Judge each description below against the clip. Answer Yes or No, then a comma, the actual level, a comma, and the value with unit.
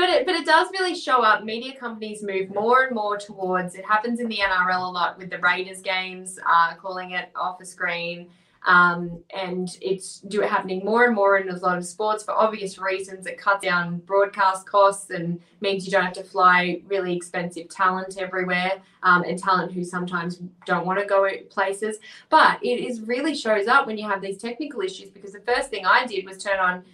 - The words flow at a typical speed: No, fast, 215 wpm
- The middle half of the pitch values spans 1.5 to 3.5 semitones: Yes, narrow, 2.6 semitones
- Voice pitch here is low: No, high, 190 Hz